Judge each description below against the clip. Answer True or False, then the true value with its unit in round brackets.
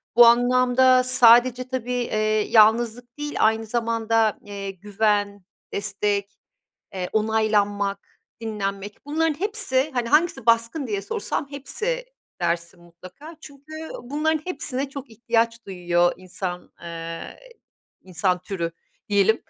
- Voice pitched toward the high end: True (225 Hz)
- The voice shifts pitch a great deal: False (4.3 semitones)